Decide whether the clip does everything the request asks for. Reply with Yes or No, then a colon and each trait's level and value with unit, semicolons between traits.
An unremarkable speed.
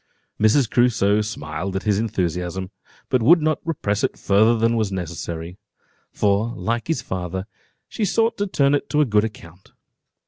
Yes: average, 165 wpm